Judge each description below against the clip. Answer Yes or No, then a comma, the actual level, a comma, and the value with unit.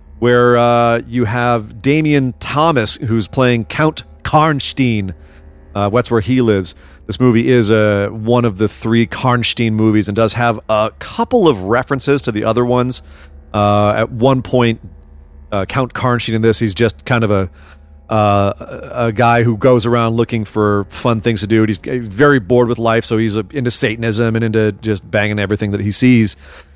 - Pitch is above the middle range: No, low, 115 Hz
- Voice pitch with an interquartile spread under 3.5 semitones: Yes, average, 2.9 semitones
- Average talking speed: Yes, average, 180 wpm